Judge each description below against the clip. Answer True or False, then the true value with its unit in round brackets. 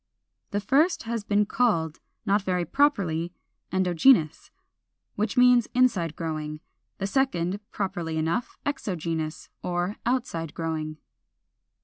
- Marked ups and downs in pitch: True (6.2 semitones)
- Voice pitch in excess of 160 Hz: True (185 Hz)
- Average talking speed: False (105 wpm)